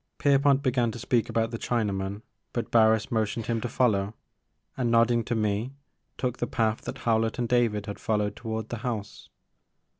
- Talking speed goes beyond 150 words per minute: Yes, average, 175 wpm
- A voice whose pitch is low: Yes, low, 115 Hz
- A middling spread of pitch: No, narrow, 2.0 semitones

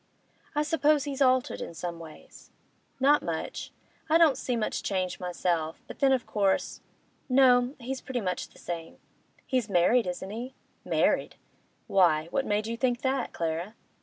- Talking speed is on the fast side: No, average, 160 wpm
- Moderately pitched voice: No, high, 230 Hz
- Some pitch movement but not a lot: No, wide, 6.8 semitones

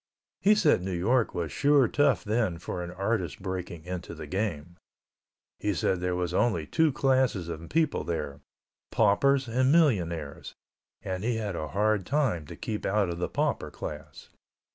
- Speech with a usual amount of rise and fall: No, wide, 6.4 semitones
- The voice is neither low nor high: No, very low, 95 Hz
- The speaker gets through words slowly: No, average, 165 wpm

